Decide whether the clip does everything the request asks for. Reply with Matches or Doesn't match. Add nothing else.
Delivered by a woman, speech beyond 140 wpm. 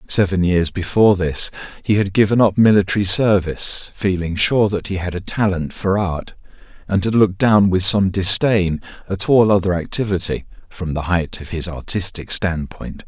Doesn't match